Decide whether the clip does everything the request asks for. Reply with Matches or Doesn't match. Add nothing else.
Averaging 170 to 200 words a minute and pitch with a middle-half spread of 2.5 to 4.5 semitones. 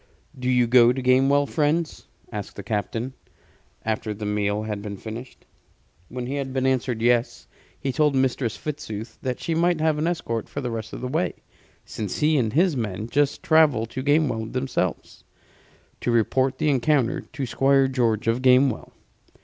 Matches